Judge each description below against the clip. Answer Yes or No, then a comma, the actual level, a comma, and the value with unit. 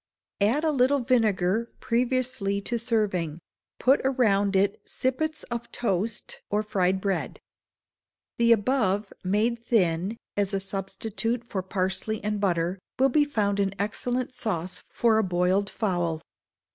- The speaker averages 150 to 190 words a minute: No, slow, 135 wpm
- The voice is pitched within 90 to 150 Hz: No, high, 210 Hz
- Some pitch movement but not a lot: Yes, average, 3.7 semitones